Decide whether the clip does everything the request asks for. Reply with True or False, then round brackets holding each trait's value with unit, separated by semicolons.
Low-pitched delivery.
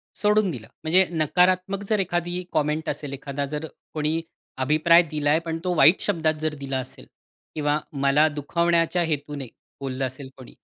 False (155 Hz)